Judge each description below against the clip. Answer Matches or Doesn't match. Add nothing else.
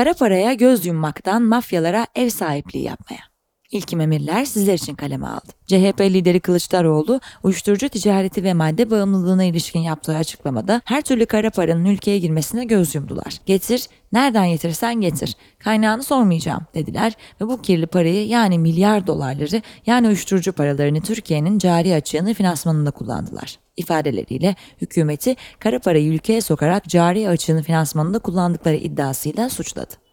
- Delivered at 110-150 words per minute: Matches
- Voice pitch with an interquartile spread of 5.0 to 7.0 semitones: Matches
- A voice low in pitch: Doesn't match